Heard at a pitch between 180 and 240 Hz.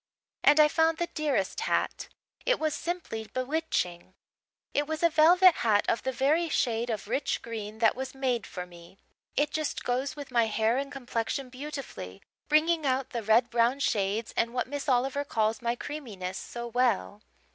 No: very high, 255 Hz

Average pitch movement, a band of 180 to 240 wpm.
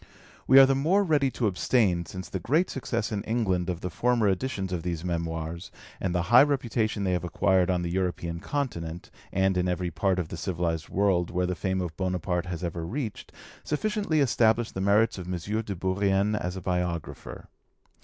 Yes: average, 4.4 semitones; average, 195 wpm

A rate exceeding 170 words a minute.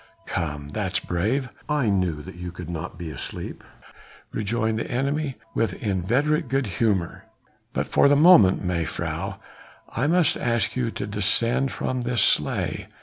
No: average, 145 wpm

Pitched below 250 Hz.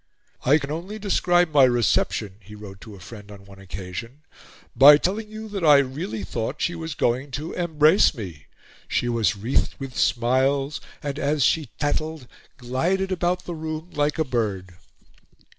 Yes: medium, 140 Hz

